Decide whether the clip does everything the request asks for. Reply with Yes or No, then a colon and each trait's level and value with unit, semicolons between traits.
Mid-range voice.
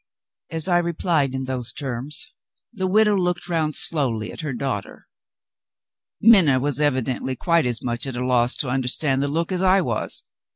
Yes: medium, 145 Hz